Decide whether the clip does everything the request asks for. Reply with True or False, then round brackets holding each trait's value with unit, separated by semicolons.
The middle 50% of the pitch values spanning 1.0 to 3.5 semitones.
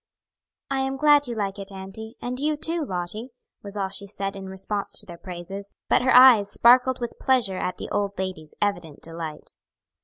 False (4.7 semitones)